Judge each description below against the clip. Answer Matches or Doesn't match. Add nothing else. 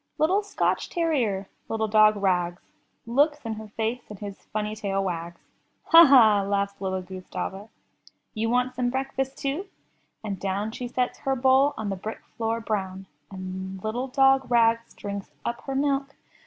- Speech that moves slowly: Doesn't match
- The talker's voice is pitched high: Matches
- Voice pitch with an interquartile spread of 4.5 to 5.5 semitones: Matches